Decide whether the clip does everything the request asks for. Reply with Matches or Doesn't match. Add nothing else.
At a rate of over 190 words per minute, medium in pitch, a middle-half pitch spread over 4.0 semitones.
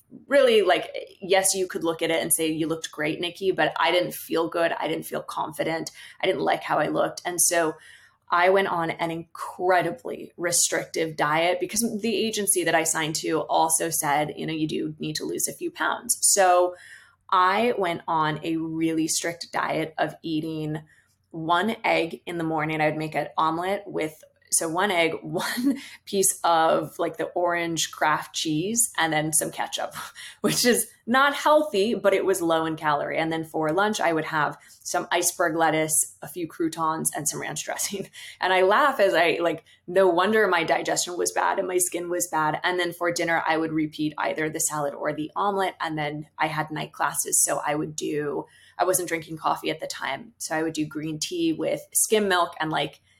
Doesn't match